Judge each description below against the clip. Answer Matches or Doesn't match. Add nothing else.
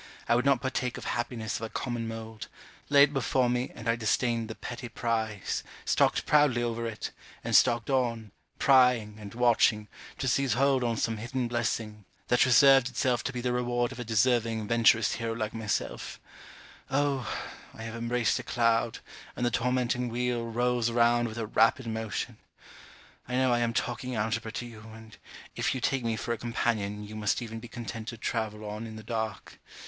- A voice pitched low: Matches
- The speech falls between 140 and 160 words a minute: Doesn't match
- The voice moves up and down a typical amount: Doesn't match